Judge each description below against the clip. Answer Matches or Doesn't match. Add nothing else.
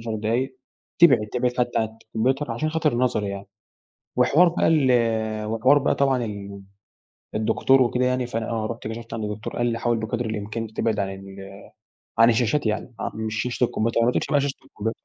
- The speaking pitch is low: Matches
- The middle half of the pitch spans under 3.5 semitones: Matches